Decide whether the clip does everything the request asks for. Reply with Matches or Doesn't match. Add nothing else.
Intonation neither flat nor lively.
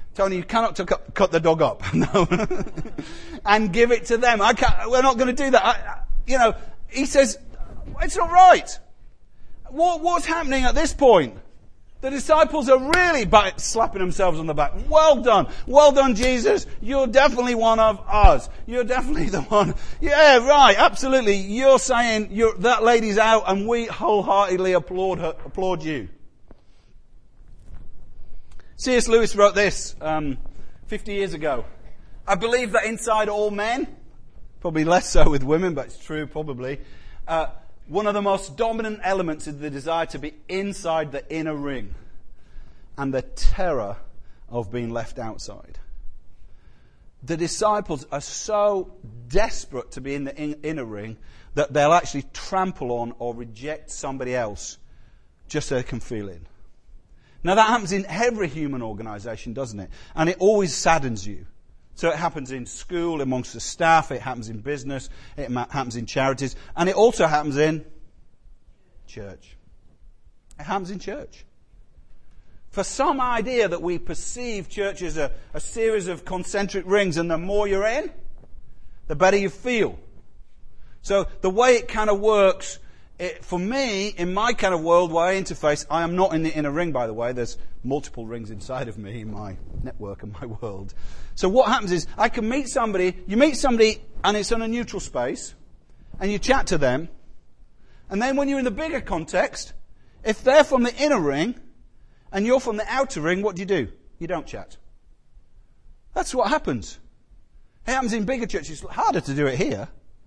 Doesn't match